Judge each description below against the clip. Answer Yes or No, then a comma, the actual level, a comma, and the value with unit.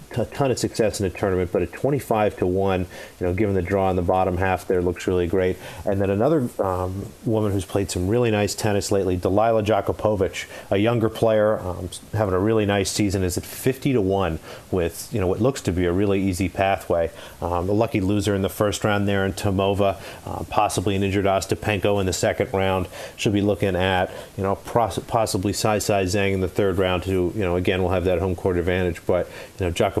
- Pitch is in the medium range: No, low, 100 Hz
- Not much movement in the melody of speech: Yes, narrow, 2.2 semitones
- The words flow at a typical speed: No, fast, 230 wpm